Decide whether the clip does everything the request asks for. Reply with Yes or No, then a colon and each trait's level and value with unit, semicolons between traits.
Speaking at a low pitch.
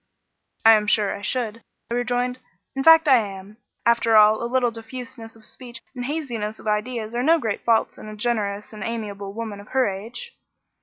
No: high, 230 Hz